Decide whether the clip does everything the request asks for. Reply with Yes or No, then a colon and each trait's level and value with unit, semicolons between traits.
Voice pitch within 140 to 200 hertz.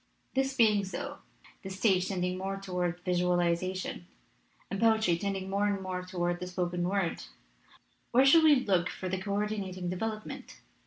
Yes: high, 190 Hz